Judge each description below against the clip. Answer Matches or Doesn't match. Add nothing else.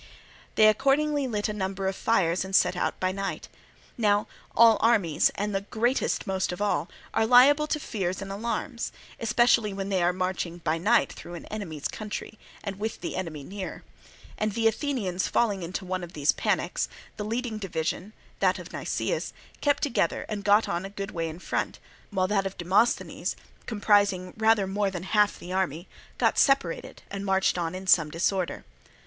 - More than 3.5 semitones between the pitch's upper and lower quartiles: Doesn't match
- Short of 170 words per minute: Doesn't match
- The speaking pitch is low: Doesn't match